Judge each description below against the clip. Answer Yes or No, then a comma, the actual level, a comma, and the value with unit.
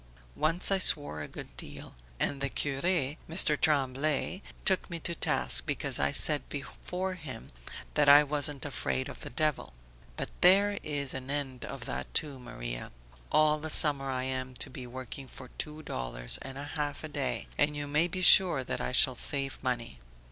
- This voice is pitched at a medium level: Yes, medium, 145 Hz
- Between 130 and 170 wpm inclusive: No, average, 185 wpm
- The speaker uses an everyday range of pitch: Yes, average, 3.0 semitones